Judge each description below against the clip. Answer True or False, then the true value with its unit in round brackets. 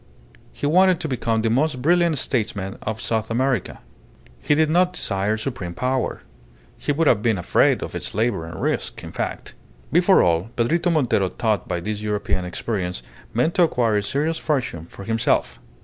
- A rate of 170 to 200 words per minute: True (175 wpm)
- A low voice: True (115 Hz)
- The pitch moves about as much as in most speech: False (6.7 semitones)